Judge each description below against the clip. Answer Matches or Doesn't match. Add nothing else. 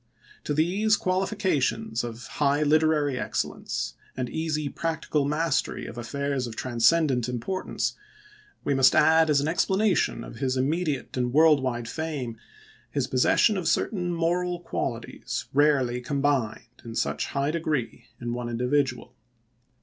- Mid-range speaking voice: Matches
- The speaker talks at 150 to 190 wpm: Doesn't match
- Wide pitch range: Doesn't match